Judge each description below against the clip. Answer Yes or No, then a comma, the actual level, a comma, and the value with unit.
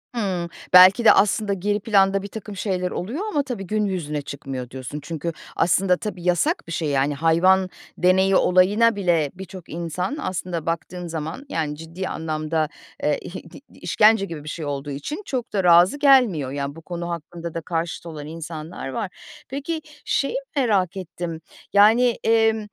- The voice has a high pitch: No, medium, 180 Hz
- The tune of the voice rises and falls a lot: No, average, 4.2 semitones